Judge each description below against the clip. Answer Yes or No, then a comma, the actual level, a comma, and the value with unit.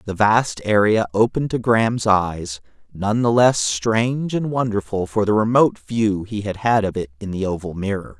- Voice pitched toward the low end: Yes, low, 105 Hz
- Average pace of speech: Yes, average, 190 wpm